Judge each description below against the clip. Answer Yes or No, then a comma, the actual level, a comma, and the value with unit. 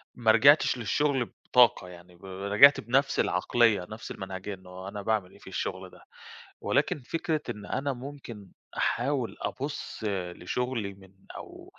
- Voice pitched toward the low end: Yes, low, 110 Hz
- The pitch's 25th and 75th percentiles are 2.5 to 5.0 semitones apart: No, wide, 5.5 semitones